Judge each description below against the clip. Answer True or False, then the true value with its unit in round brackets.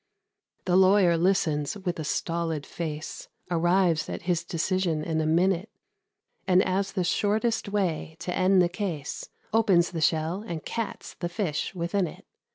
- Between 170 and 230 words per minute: False (155 wpm)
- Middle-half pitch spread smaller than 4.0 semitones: True (2.8 semitones)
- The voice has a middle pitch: True (175 Hz)